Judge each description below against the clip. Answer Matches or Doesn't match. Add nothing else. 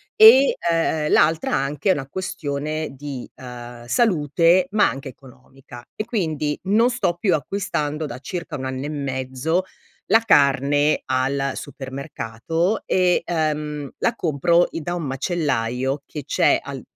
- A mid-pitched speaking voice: Matches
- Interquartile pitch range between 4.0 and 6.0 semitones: Matches